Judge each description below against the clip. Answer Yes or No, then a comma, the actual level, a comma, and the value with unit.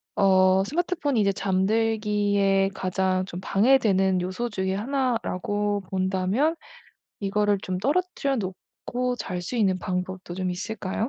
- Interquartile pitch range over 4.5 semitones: No, average, 3.1 semitones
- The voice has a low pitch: No, high, 195 Hz